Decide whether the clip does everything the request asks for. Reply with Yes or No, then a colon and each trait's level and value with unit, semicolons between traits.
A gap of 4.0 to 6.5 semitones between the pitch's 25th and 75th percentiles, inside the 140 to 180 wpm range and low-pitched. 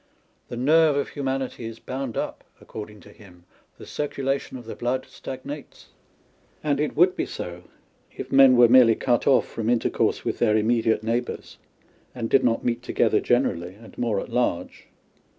No: average, 3.2 semitones; average, 170 wpm; low, 120 Hz